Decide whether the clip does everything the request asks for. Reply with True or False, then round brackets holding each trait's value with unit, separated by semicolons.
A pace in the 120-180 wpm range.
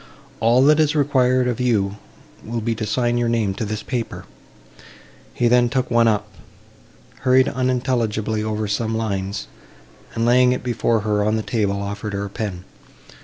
True (170 wpm)